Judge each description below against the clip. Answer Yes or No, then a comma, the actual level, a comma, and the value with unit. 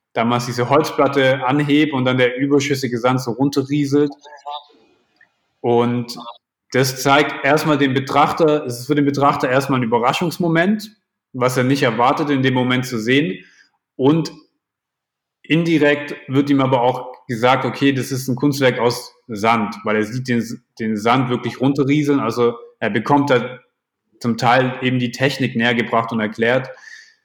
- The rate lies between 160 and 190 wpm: No, average, 150 wpm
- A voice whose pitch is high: No, low, 130 Hz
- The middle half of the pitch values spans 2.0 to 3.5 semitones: Yes, average, 2.9 semitones